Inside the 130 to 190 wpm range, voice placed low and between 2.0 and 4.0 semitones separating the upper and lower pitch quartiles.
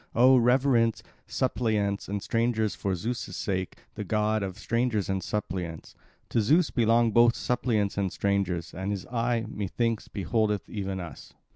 Yes: average, 145 wpm; low, 110 Hz; average, 3.2 semitones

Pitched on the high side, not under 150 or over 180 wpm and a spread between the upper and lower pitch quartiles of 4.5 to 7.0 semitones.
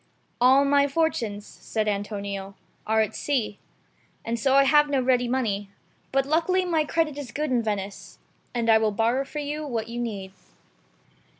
Yes: high, 245 Hz; average, 170 wpm; average, 4.9 semitones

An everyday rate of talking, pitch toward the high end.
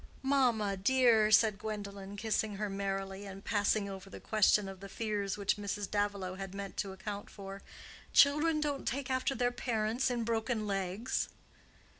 Yes: average, 160 wpm; high, 205 Hz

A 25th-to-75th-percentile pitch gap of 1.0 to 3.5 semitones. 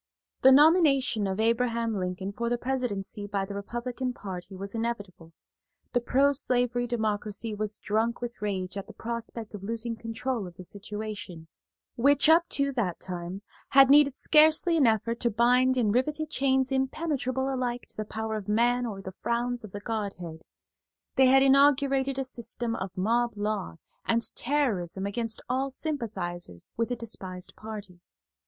No: average, 4.2 semitones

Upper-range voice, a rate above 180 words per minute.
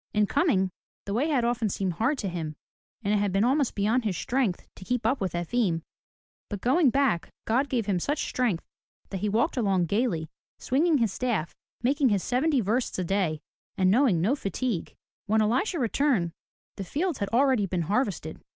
Yes: high, 220 Hz; average, 190 wpm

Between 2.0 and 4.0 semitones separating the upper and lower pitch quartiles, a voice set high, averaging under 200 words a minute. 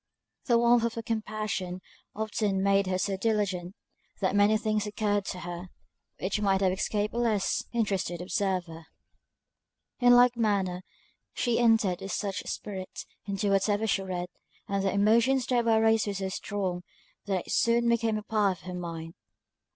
Yes: average, 2.8 semitones; high, 205 Hz; average, 160 wpm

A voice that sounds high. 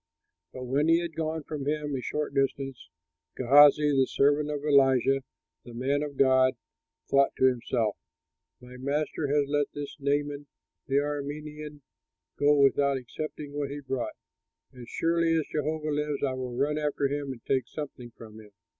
No: medium, 145 Hz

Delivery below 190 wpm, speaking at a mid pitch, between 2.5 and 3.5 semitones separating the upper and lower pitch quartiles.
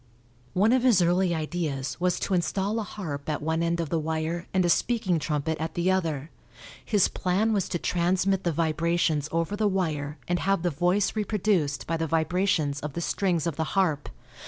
No: average, 195 wpm; medium, 170 Hz; average, 3.1 semitones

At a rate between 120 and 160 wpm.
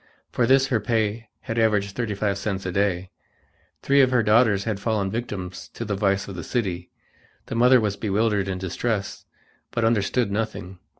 No: average, 180 wpm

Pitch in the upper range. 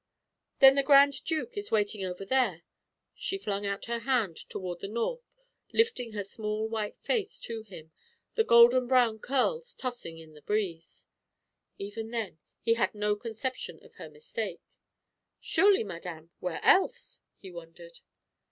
Yes: high, 220 Hz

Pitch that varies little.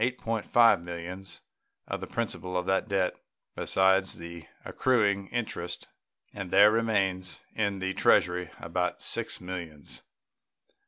Yes: narrow, 2.3 semitones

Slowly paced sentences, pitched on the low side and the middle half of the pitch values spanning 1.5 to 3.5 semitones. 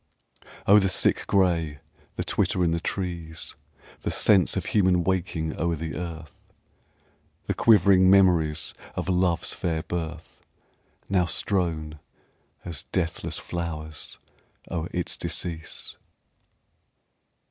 Yes: slow, 110 wpm; very low, 85 Hz; narrow, 2.5 semitones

